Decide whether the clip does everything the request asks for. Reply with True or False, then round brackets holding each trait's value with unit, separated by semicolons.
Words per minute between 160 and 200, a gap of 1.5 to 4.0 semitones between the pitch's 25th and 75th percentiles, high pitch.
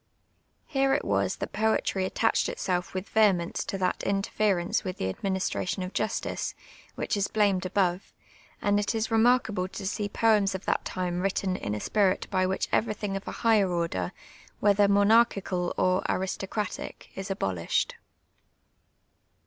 False (150 wpm; 2.4 semitones; 195 Hz)